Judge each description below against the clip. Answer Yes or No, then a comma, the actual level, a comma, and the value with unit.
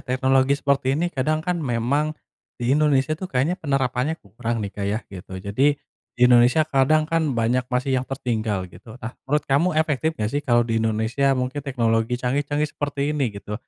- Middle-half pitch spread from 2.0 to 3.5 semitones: No, average, 3.9 semitones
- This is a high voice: No, low, 130 Hz